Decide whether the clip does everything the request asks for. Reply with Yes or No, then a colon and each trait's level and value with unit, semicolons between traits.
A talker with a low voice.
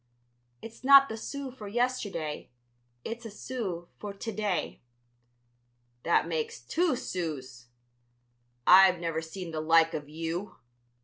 No: medium, 185 Hz